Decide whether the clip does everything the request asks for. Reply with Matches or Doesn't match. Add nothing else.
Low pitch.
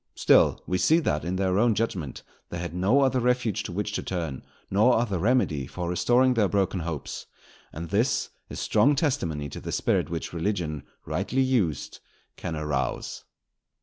Matches